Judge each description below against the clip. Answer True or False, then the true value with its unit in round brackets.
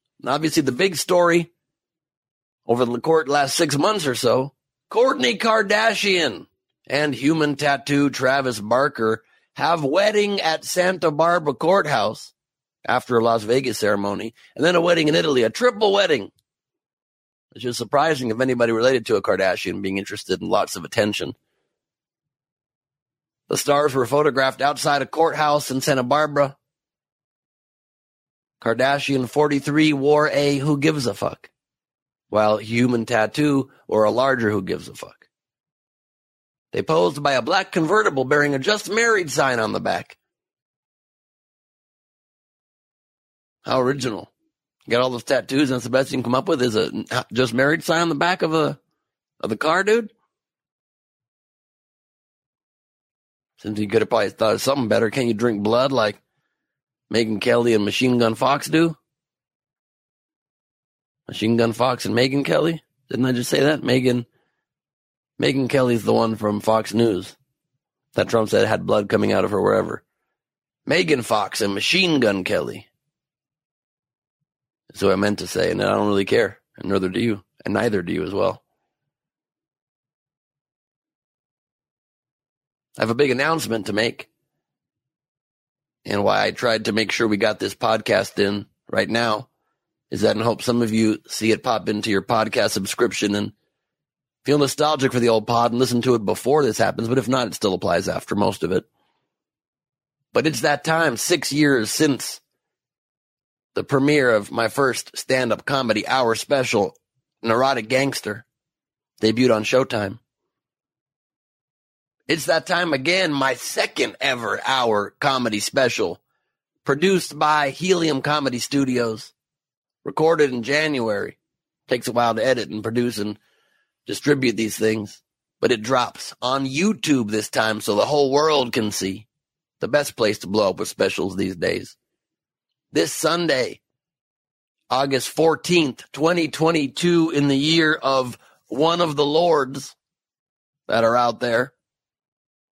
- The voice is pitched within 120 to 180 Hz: True (135 Hz)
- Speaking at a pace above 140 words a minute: True (150 wpm)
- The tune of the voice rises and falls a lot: False (4.7 semitones)